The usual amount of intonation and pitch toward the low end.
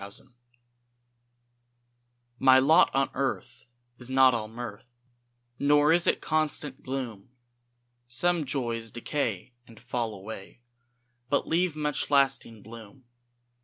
Yes: average, 4.0 semitones; low, 130 Hz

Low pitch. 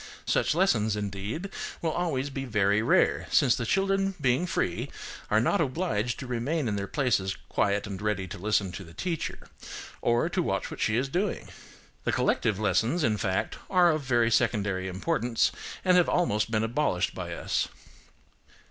Yes: low, 120 Hz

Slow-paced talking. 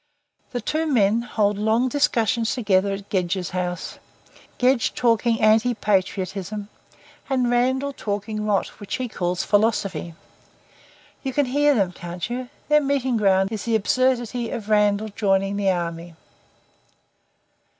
Yes: slow, 130 wpm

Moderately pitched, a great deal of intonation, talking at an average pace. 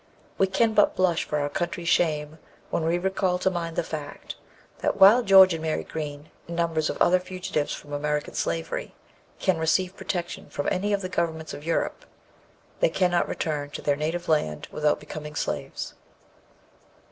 No: medium, 165 Hz; average, 3.4 semitones; average, 170 wpm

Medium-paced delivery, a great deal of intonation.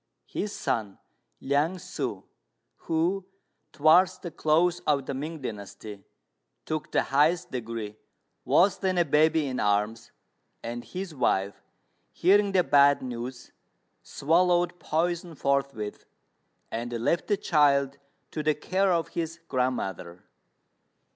No: slow, 120 wpm; wide, 6.1 semitones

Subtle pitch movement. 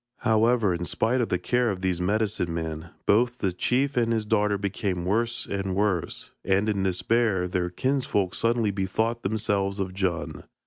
No: average, 3.7 semitones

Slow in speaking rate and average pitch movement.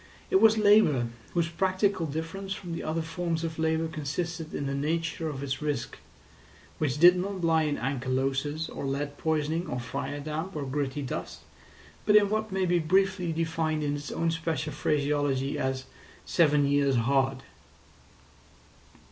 No: average, 155 wpm; average, 3.2 semitones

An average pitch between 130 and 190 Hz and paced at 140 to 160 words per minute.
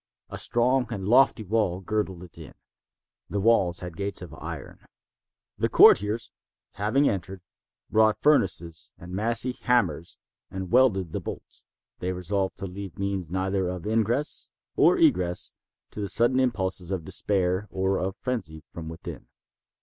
No: very low, 95 Hz; average, 145 wpm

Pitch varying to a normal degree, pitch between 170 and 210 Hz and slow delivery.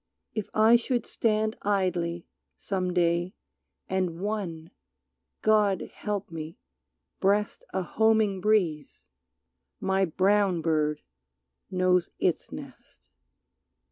Yes: average, 3.6 semitones; high, 190 Hz; slow, 95 wpm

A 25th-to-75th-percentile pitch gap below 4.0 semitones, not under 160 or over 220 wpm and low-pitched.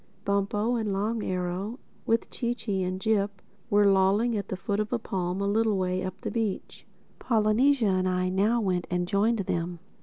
No: average, 3.0 semitones; average, 185 wpm; high, 200 Hz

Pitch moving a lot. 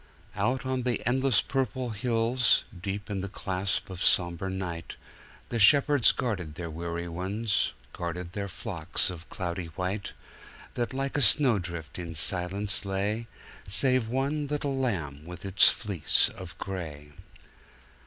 Yes: wide, 5.7 semitones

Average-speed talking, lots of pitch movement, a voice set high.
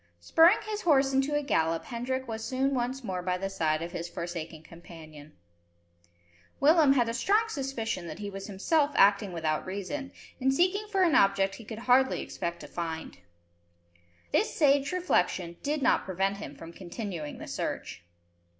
Yes: average, 170 wpm; wide, 8.0 semitones; high, 220 Hz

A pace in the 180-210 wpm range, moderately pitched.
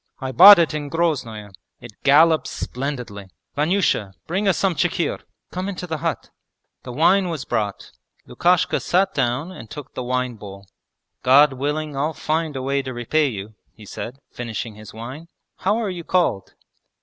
No: average, 165 wpm; medium, 145 Hz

